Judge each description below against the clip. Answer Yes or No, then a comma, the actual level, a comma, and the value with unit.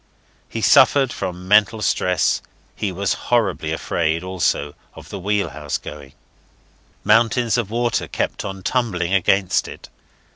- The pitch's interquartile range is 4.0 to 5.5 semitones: Yes, average, 4.5 semitones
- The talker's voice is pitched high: No, very low, 95 Hz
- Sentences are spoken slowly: Yes, slow, 130 wpm